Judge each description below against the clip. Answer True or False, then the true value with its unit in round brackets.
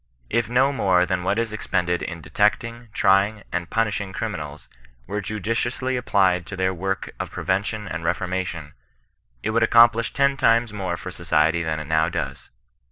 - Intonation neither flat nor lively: True (4.4 semitones)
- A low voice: True (95 Hz)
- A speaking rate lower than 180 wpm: True (165 wpm)